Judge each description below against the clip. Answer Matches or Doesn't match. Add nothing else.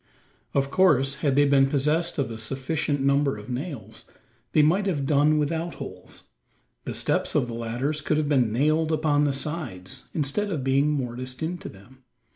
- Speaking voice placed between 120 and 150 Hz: Matches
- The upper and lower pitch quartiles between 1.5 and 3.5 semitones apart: Matches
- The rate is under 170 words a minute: Doesn't match